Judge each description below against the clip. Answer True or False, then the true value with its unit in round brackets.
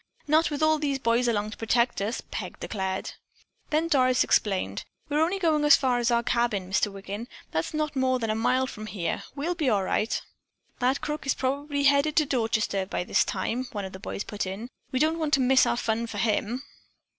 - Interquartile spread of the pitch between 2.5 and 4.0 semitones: False (5.1 semitones)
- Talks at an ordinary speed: False (215 wpm)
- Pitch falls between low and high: False (250 Hz)